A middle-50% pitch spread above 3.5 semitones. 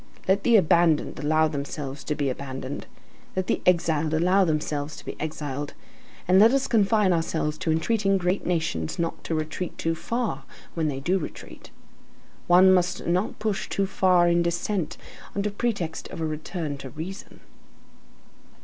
Yes: average, 3.9 semitones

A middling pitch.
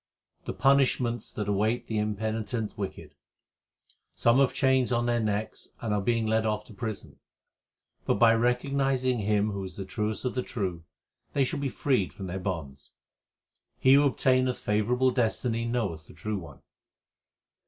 No: low, 110 Hz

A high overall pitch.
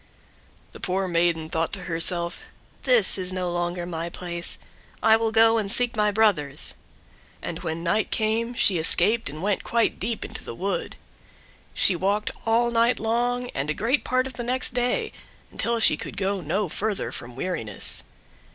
Yes: high, 200 Hz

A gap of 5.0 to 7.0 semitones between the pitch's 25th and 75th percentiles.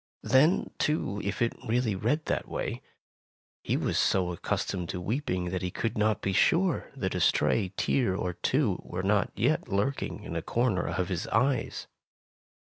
Yes: wide, 5.4 semitones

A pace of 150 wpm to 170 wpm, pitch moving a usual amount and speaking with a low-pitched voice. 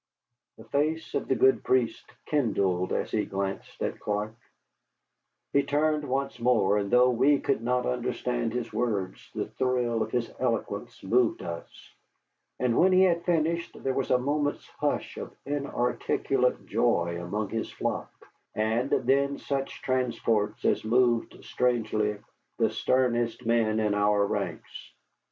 No: average, 140 wpm; average, 3.8 semitones; low, 120 Hz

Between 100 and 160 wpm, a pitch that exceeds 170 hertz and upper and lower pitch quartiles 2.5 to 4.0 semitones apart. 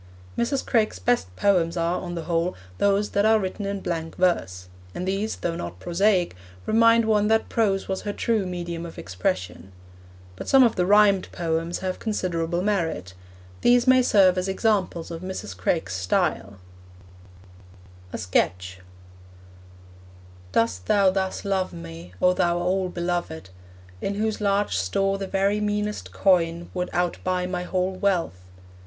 Yes: average, 150 wpm; medium, 185 Hz; average, 3.4 semitones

